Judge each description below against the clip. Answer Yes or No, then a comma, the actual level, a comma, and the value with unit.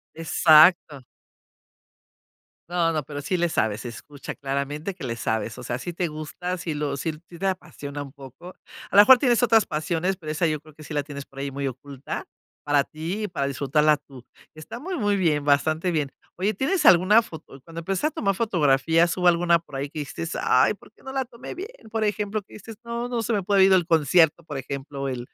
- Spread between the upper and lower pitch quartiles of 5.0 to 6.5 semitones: Yes, average, 5.3 semitones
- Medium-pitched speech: Yes, medium, 160 Hz